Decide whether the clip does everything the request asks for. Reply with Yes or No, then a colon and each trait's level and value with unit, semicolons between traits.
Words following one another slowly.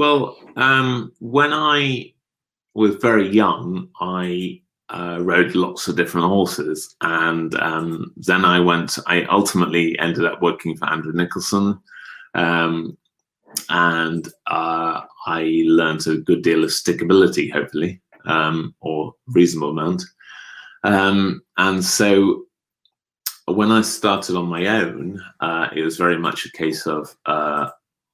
Yes: slow, 130 wpm